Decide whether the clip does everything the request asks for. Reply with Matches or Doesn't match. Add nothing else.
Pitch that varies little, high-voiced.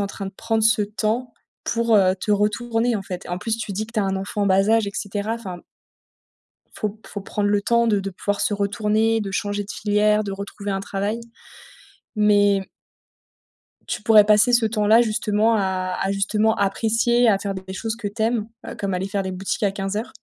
Matches